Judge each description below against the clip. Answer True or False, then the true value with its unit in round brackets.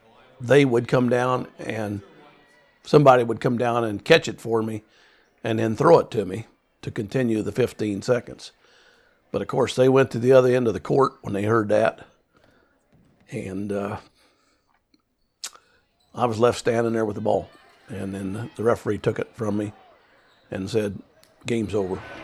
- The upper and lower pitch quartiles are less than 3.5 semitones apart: True (2.9 semitones)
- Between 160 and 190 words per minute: True (170 wpm)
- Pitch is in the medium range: False (115 Hz)